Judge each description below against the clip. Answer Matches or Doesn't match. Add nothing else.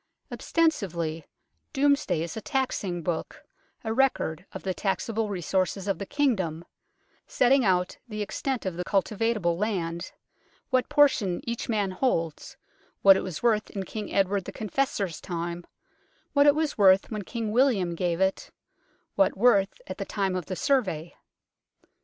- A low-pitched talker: Doesn't match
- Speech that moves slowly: Doesn't match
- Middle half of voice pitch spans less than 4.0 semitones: Doesn't match